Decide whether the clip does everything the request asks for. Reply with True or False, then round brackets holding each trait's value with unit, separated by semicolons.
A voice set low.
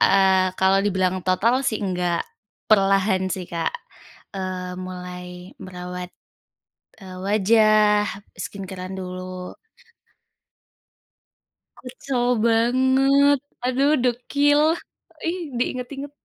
False (195 Hz)